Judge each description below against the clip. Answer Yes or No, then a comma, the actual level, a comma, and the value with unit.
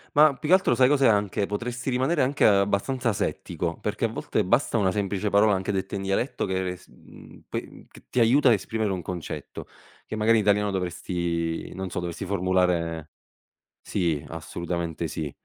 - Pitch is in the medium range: No, low, 100 Hz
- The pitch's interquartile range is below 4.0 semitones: No, average, 4.3 semitones